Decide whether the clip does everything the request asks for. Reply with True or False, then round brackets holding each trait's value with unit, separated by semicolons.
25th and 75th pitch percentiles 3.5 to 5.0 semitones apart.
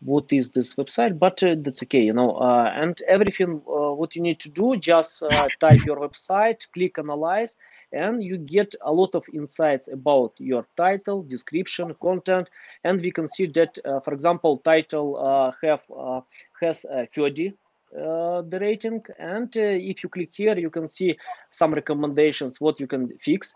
True (4.2 semitones)